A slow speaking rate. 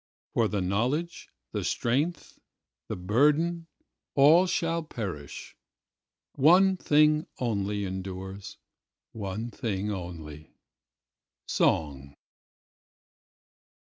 Yes: slow, 65 wpm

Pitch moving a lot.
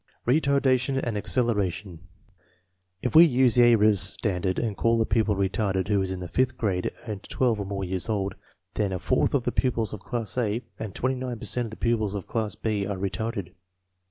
No: average, 3.7 semitones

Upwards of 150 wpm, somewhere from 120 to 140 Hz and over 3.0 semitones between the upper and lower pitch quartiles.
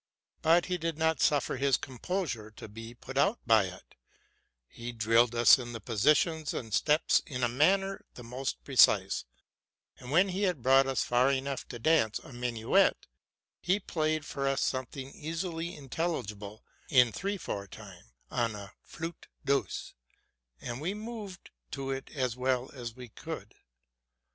Yes: average, 160 wpm; low, 135 Hz; wide, 5.4 semitones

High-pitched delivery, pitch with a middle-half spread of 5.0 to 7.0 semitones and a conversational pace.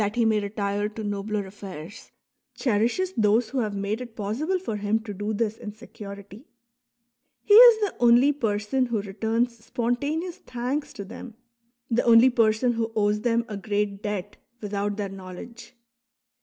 No: high, 220 Hz; average, 2.9 semitones; average, 155 wpm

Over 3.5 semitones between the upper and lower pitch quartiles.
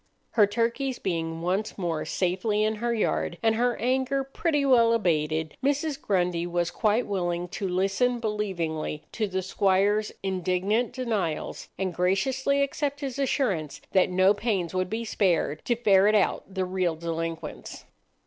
Yes: average, 5.0 semitones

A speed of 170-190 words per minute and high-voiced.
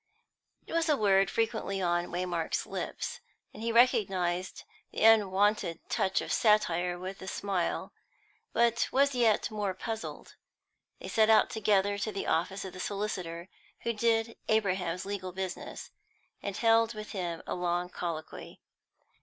No: average, 145 wpm; high, 195 Hz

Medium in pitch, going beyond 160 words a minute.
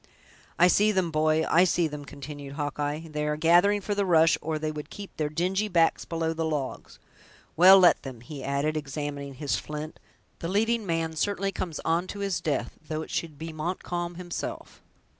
Yes: medium, 160 Hz; average, 190 wpm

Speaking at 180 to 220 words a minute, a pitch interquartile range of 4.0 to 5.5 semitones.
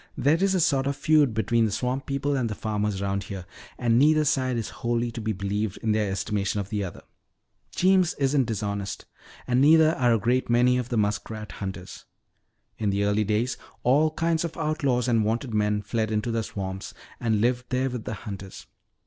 Yes: average, 200 wpm; average, 4.3 semitones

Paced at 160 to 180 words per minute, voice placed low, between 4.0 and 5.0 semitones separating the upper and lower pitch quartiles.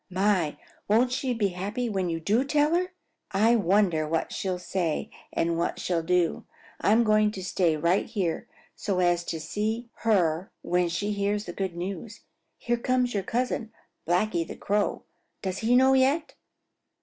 No: average, 165 wpm; high, 200 Hz; average, 4.6 semitones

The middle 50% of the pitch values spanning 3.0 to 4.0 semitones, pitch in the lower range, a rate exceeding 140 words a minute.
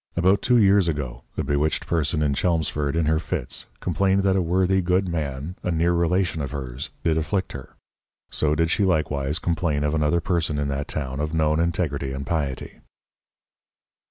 Yes: average, 3.5 semitones; very low, 80 Hz; average, 180 wpm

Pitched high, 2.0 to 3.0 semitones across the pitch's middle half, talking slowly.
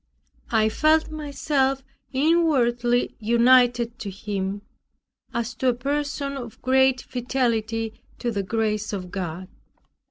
No: high, 240 Hz; average, 3.6 semitones; slow, 115 wpm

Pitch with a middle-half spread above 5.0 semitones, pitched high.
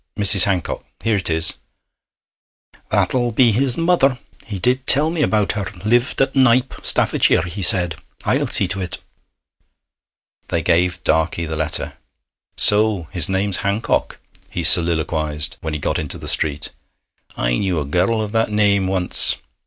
No: wide, 5.5 semitones; low, 100 Hz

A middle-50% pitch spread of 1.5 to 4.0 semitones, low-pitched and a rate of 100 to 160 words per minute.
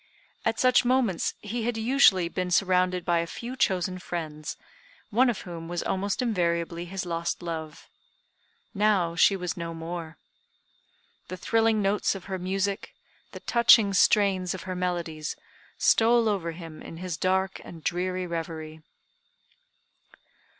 No: average, 3.1 semitones; medium, 185 Hz; average, 140 wpm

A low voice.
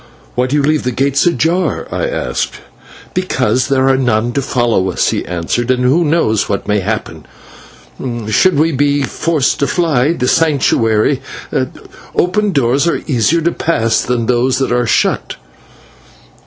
Yes: low, 130 Hz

